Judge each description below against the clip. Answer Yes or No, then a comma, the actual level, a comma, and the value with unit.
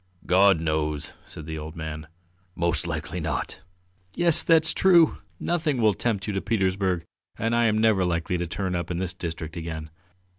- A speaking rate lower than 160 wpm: No, average, 175 wpm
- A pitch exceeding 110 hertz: No, very low, 90 Hz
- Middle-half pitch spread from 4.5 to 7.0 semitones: Yes, average, 5.2 semitones